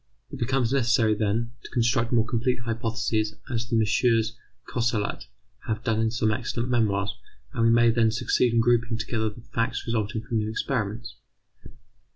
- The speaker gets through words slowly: No, average, 165 wpm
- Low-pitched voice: Yes, low, 115 Hz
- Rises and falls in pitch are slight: Yes, narrow, 1.3 semitones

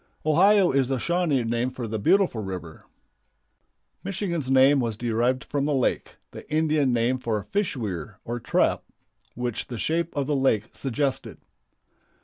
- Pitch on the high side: No, low, 130 Hz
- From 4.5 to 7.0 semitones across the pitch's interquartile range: Yes, average, 4.8 semitones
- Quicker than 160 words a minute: No, average, 150 wpm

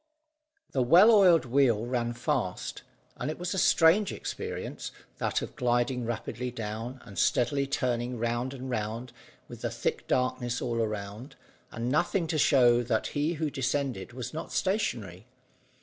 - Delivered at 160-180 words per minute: No, average, 150 wpm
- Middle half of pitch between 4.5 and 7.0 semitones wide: No, average, 3.6 semitones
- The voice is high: No, low, 125 Hz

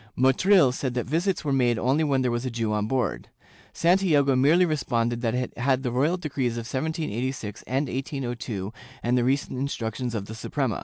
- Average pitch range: Yes, average, 3.2 semitones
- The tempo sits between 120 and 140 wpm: No, average, 190 wpm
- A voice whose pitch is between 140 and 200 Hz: No, low, 130 Hz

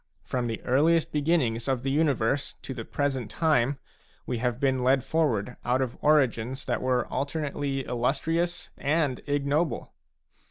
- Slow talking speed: No, average, 150 wpm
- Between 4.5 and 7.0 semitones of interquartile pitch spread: No, average, 3.2 semitones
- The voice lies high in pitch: No, low, 135 Hz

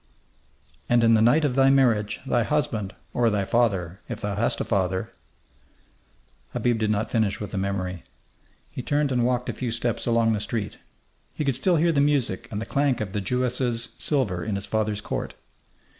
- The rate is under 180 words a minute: No, average, 195 wpm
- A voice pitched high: No, low, 115 Hz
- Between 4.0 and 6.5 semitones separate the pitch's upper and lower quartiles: No, average, 3.6 semitones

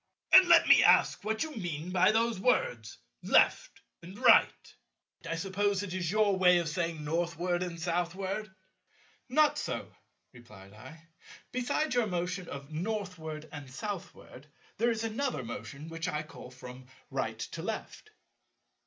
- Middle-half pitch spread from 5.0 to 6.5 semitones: Yes, average, 5.3 semitones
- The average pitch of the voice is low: No, medium, 175 Hz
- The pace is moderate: Yes, average, 145 wpm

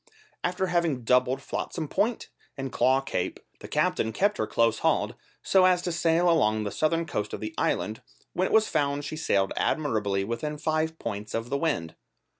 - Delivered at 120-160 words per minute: No, average, 185 wpm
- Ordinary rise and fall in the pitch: No, wide, 7.0 semitones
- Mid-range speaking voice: Yes, medium, 145 Hz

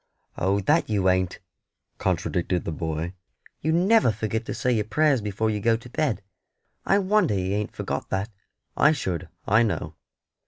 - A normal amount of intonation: No, wide, 6.6 semitones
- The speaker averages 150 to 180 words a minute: Yes, average, 165 wpm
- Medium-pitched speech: No, low, 105 Hz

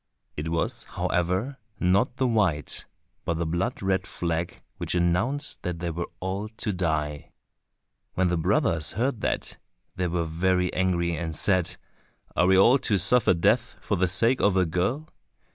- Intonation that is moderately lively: Yes, average, 3.3 semitones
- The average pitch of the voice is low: Yes, very low, 90 Hz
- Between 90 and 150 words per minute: No, average, 160 wpm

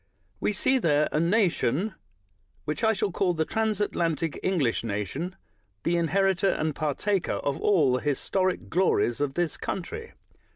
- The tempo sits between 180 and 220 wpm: No, average, 150 wpm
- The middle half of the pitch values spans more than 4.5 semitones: Yes, average, 5.0 semitones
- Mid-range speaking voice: Yes, medium, 170 Hz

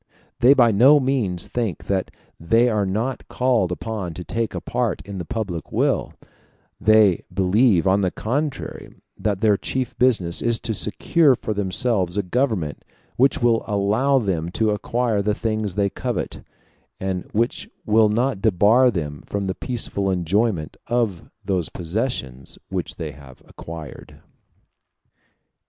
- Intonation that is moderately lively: Yes, average, 4.4 semitones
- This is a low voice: Yes, low, 105 Hz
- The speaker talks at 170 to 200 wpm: No, average, 145 wpm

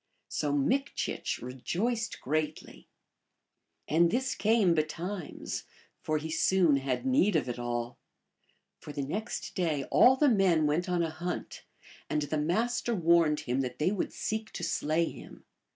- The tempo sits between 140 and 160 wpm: Yes, average, 150 wpm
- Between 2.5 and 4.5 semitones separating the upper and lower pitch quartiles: No, wide, 5.6 semitones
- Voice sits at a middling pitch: Yes, medium, 165 Hz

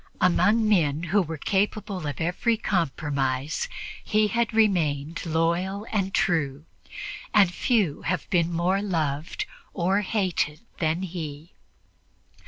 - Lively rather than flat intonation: No, average, 4.6 semitones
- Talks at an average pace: No, slow, 115 wpm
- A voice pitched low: No, medium, 175 Hz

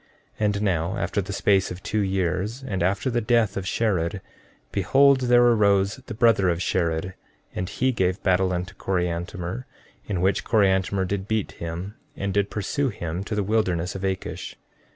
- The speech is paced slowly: No, average, 175 wpm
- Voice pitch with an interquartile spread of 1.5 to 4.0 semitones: Yes, average, 2.8 semitones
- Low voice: Yes, very low, 95 Hz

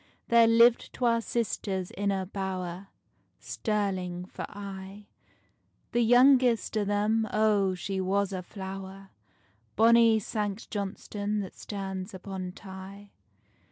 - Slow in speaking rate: Yes, slow, 115 wpm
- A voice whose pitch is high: Yes, high, 200 Hz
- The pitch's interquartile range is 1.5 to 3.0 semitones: Yes, narrow, 2.4 semitones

